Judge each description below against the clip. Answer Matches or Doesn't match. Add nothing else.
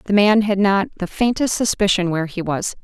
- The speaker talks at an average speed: Doesn't match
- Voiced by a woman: Matches